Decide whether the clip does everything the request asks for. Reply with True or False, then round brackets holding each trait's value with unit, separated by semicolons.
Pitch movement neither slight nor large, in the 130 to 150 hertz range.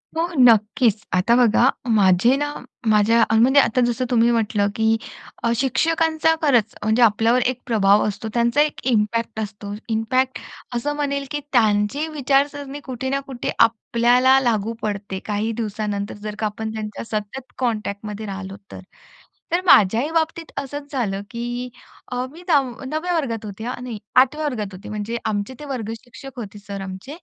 False (4.0 semitones; 235 Hz)